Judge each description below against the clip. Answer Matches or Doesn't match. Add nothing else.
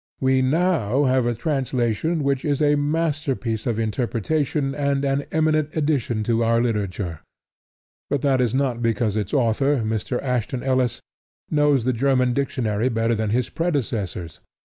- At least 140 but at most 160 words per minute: Matches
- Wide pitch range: Doesn't match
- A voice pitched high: Doesn't match